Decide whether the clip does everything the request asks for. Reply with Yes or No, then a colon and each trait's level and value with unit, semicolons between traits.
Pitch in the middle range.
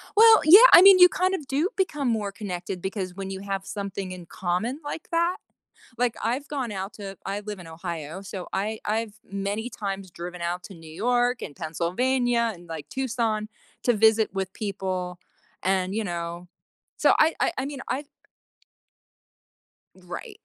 No: high, 200 Hz